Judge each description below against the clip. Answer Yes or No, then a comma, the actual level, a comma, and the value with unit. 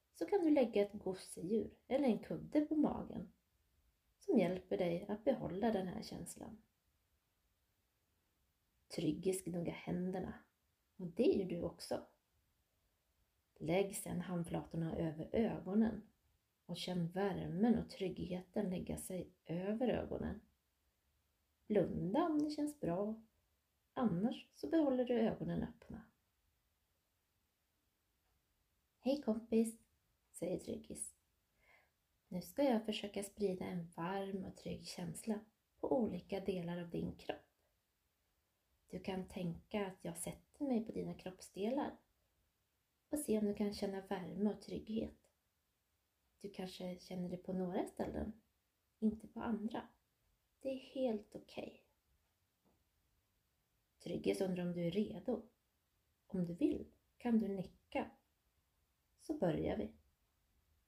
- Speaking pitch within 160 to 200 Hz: Yes, medium, 185 Hz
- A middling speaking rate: No, slow, 120 wpm